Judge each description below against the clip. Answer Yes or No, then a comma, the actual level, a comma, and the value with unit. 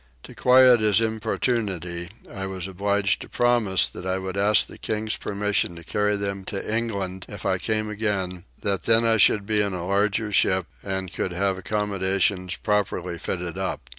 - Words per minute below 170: No, average, 175 wpm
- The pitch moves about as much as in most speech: No, narrow, 2.3 semitones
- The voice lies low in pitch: Yes, low, 100 Hz